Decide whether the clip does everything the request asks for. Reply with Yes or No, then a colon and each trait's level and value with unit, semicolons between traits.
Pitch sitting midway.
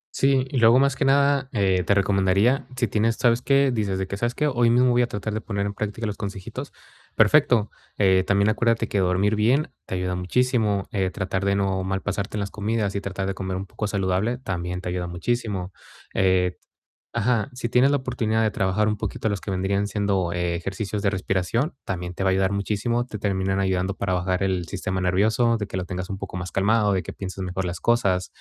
No: low, 100 Hz